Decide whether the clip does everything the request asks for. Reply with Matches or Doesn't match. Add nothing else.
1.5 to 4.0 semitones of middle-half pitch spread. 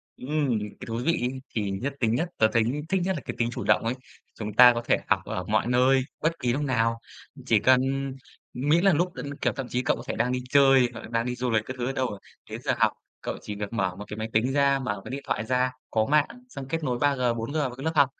Matches